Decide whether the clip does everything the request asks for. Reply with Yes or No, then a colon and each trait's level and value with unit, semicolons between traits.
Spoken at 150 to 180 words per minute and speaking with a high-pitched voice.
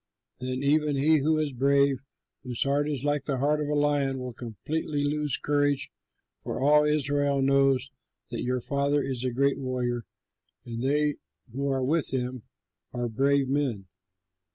No: average, 160 wpm; medium, 140 Hz